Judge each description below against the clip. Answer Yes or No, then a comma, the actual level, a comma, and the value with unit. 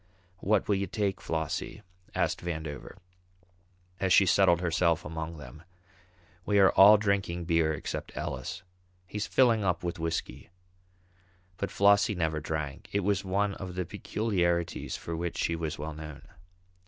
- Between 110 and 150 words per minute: Yes, average, 145 wpm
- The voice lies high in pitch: No, very low, 85 Hz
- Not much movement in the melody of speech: No, average, 3.7 semitones